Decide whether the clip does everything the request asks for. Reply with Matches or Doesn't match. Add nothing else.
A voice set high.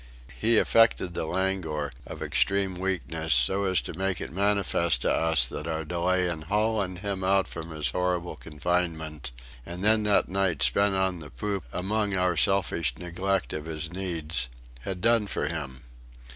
Doesn't match